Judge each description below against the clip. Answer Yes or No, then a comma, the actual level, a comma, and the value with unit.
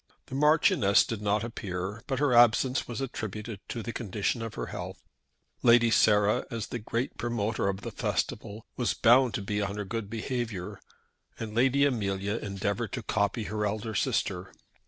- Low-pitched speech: Yes, low, 110 Hz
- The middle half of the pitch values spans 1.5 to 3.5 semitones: Yes, average, 2.8 semitones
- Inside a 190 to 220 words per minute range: No, average, 170 wpm